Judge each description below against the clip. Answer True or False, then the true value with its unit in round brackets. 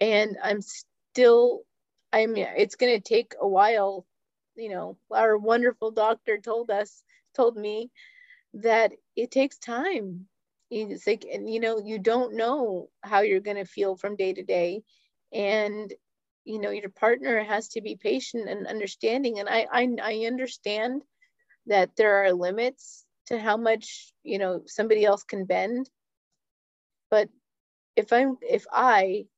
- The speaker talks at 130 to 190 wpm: True (150 wpm)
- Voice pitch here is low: False (220 Hz)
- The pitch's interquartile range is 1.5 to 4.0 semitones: True (3.3 semitones)